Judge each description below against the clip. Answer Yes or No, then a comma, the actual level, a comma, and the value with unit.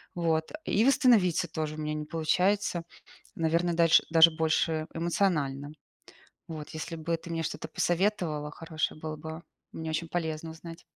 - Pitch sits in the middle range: Yes, medium, 165 Hz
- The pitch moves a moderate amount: No, narrow, 1.6 semitones